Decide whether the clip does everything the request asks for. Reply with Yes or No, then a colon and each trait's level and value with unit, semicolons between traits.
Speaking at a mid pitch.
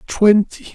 No: high, 205 Hz